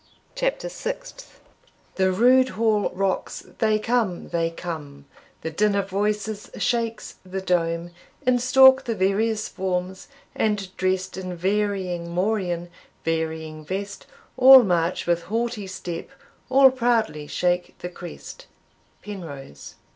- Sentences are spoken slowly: Yes, slow, 120 wpm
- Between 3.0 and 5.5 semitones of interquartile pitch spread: Yes, average, 4.3 semitones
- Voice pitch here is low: No, high, 190 Hz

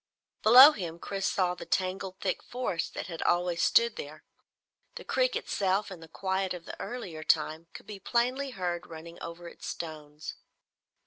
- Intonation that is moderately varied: Yes, average, 3.8 semitones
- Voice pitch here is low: No, medium, 185 Hz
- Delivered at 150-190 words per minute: Yes, average, 170 wpm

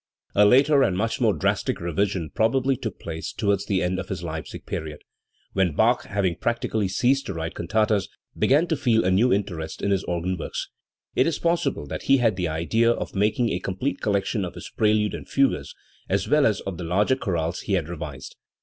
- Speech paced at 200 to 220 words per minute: Yes, fast, 205 wpm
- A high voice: No, low, 100 Hz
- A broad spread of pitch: No, average, 4.8 semitones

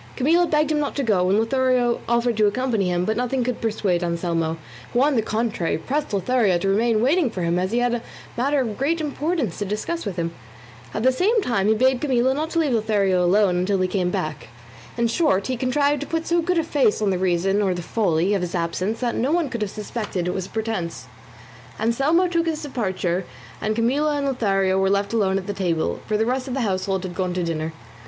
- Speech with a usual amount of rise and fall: No, wide, 5.8 semitones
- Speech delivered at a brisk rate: Yes, fast, 235 wpm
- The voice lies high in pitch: Yes, high, 220 Hz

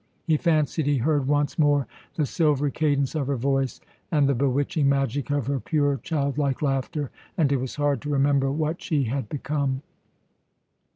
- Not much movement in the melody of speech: Yes, narrow, 1.5 semitones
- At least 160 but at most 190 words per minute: Yes, average, 170 wpm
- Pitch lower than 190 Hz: Yes, medium, 140 Hz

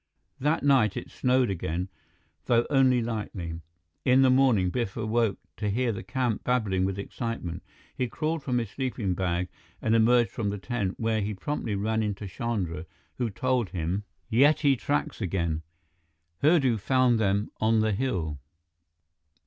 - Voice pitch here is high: No, low, 110 Hz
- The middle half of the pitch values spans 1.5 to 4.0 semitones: No, average, 4.6 semitones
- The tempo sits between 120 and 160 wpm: Yes, average, 150 wpm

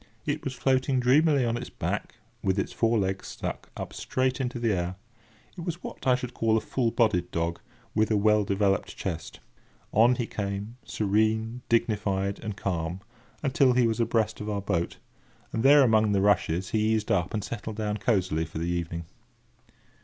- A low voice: Yes, low, 110 Hz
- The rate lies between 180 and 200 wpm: Yes, average, 185 wpm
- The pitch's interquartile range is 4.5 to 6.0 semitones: No, average, 3.6 semitones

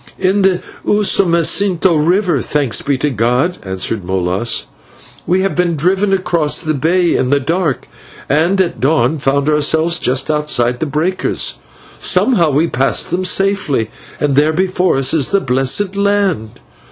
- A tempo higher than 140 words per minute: Yes, average, 155 wpm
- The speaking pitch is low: No, medium, 160 Hz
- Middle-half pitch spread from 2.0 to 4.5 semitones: No, wide, 5.4 semitones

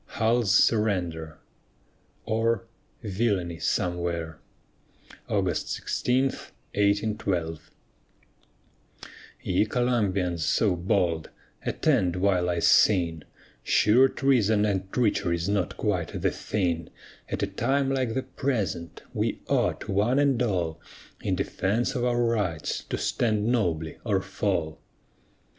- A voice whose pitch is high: No, low, 100 Hz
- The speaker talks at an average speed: No, slow, 105 wpm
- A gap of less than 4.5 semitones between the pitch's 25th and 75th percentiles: No, average, 5.0 semitones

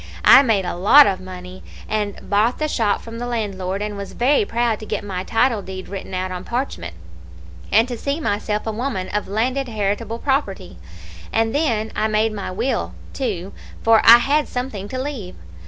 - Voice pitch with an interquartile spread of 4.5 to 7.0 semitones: No, average, 3.7 semitones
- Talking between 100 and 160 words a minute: No, average, 190 wpm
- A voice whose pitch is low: No, high, 215 Hz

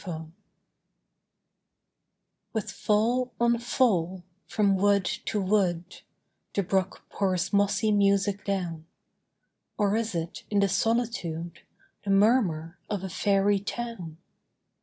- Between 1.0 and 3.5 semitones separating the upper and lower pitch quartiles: Yes, average, 2.9 semitones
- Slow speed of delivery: Yes, slow, 110 wpm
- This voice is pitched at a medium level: No, high, 200 Hz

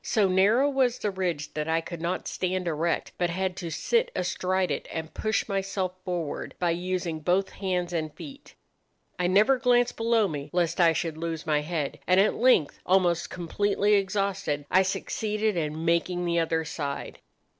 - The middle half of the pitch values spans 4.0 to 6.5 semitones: No, average, 3.3 semitones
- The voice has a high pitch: No, medium, 180 Hz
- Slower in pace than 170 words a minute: No, average, 175 wpm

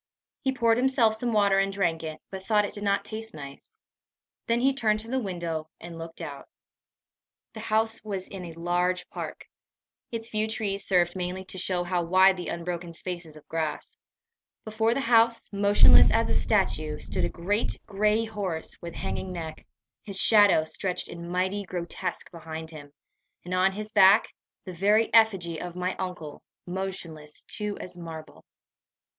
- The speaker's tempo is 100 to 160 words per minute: No, average, 170 wpm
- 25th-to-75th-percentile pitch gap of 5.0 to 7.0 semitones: No, average, 3.9 semitones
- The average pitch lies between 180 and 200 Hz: Yes, medium, 185 Hz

